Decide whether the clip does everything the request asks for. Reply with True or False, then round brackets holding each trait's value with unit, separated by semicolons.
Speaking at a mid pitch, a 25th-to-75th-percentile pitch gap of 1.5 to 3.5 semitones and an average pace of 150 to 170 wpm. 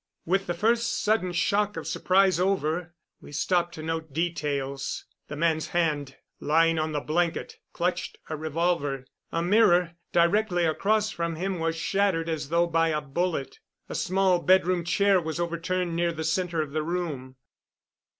True (170 Hz; 2.5 semitones; 160 wpm)